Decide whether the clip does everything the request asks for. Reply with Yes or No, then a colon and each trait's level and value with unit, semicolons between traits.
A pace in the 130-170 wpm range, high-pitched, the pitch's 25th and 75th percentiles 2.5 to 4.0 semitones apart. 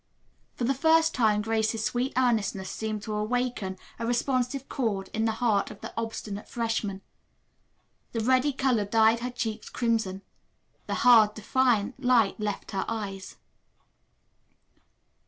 Yes: slow, 135 wpm; high, 225 Hz; average, 2.9 semitones